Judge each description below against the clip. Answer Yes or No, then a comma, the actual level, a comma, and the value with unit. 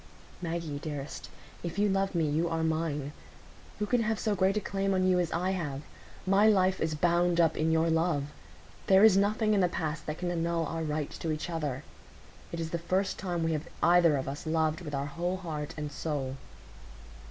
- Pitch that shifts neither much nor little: Yes, average, 3.2 semitones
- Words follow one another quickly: Yes, fast, 210 wpm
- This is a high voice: No, medium, 165 Hz